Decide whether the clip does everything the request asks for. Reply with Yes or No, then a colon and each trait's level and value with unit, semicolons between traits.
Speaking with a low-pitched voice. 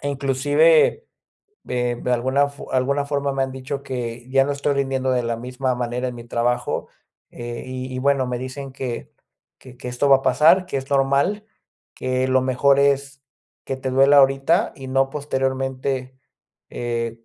Yes: low, 130 Hz